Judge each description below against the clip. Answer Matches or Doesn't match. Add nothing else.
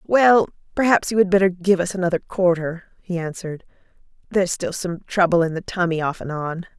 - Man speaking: Doesn't match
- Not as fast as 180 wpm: Doesn't match